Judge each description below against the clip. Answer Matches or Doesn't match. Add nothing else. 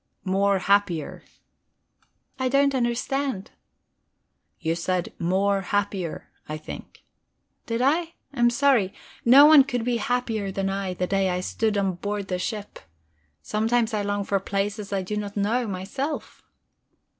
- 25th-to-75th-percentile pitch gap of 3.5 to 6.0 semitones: Matches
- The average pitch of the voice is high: Matches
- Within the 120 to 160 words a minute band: Matches